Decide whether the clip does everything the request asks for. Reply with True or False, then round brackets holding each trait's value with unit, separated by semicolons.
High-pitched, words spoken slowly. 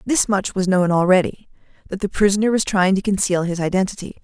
False (195 Hz; 200 wpm)